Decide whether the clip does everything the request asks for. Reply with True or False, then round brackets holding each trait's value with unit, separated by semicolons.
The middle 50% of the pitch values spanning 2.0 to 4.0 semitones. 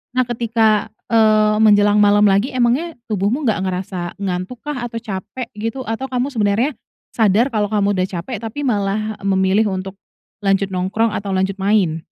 True (2.9 semitones)